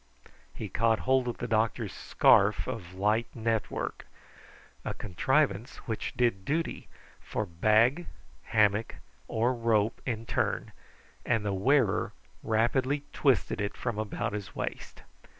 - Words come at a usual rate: No, slow, 125 wpm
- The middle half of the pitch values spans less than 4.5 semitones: Yes, average, 2.9 semitones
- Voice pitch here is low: Yes, low, 115 Hz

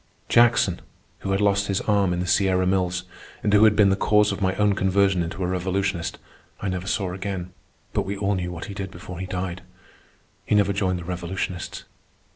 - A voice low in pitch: Yes, very low, 95 Hz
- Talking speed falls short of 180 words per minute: No, fast, 205 wpm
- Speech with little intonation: Yes, narrow, 1.7 semitones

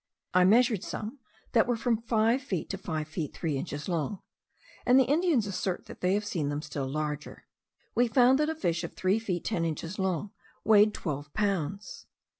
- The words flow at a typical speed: Yes, average, 190 wpm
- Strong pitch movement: Yes, wide, 6.0 semitones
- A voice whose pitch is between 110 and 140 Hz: No, high, 195 Hz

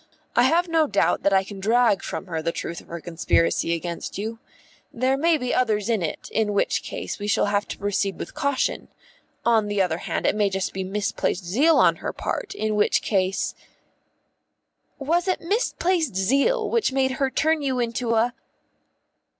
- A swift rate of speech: No, average, 190 wpm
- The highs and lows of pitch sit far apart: Yes, wide, 6.1 semitones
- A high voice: Yes, high, 225 Hz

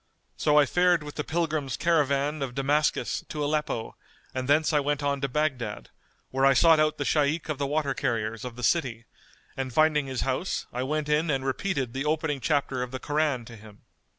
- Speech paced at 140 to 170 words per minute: No, fast, 205 wpm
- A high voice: No, medium, 145 Hz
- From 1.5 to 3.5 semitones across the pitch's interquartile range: Yes, average, 2.8 semitones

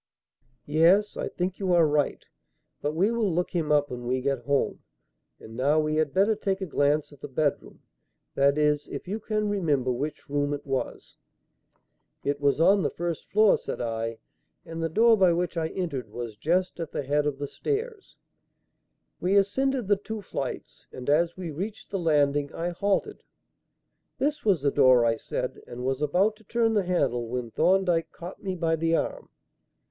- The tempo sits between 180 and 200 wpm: Yes, average, 185 wpm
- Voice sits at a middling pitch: Yes, medium, 165 Hz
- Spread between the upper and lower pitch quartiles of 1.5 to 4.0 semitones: No, average, 5.3 semitones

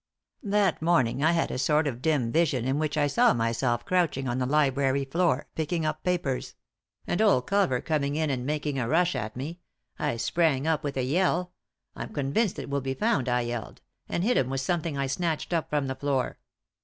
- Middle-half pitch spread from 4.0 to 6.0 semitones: Yes, average, 4.3 semitones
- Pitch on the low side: No, medium, 145 Hz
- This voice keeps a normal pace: No, fast, 215 wpm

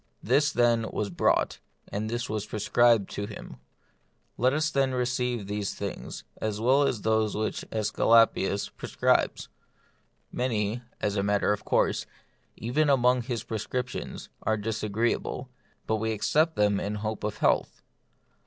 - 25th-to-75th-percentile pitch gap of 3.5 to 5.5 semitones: No, average, 3.0 semitones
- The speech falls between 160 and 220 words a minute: No, average, 145 wpm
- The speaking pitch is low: Yes, low, 110 Hz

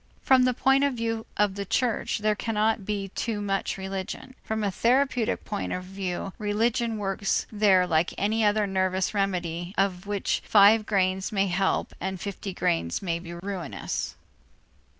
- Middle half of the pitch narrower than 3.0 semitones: Yes, narrow, 2.6 semitones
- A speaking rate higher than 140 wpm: Yes, average, 160 wpm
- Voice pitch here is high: Yes, high, 200 Hz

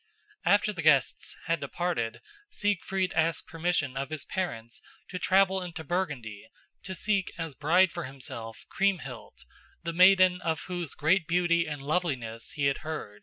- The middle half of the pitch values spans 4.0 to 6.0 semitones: Yes, average, 4.9 semitones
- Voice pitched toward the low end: No, medium, 165 Hz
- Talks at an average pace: Yes, average, 150 wpm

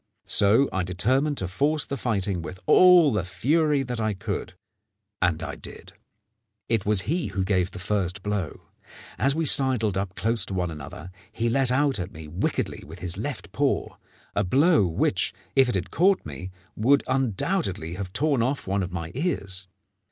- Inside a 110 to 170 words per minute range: No, average, 180 wpm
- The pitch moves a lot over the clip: Yes, wide, 6.7 semitones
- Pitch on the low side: Yes, low, 105 Hz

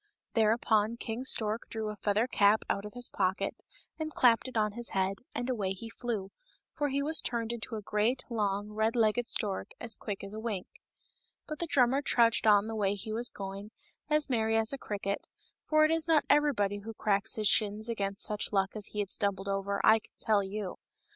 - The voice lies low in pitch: No, high, 220 Hz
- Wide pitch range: No, average, 2.9 semitones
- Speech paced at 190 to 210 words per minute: Yes, fast, 205 wpm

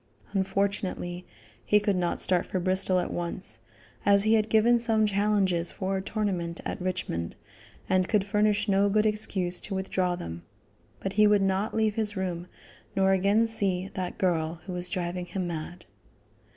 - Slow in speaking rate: No, average, 165 wpm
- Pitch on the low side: No, high, 190 Hz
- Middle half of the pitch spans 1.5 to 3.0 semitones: Yes, narrow, 2.6 semitones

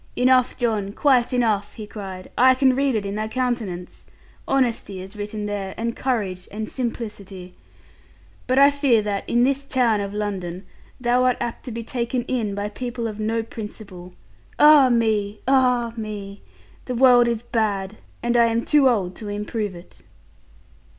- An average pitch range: Yes, average, 3.4 semitones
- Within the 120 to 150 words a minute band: No, average, 165 wpm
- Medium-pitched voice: No, high, 225 Hz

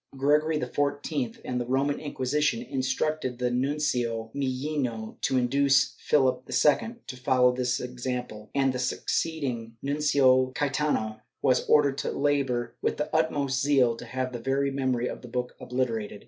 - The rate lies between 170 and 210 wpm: No, average, 150 wpm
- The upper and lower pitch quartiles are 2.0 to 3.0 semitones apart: Yes, narrow, 2.5 semitones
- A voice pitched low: Yes, low, 130 Hz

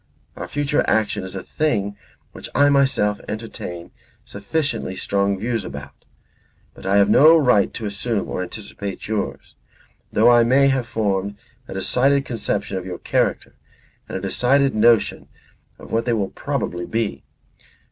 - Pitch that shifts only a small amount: No, average, 4.1 semitones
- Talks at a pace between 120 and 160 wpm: Yes, average, 155 wpm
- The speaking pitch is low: Yes, low, 110 Hz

